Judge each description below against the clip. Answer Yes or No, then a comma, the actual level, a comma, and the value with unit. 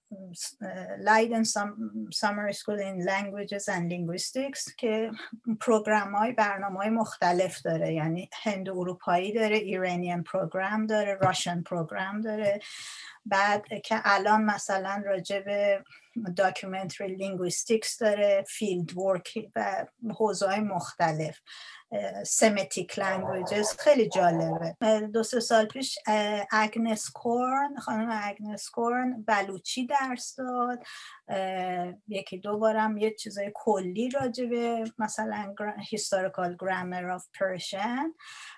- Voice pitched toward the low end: No, high, 205 Hz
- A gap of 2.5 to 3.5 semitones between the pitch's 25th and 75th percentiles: Yes, average, 2.8 semitones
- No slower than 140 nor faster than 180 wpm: No, slow, 105 wpm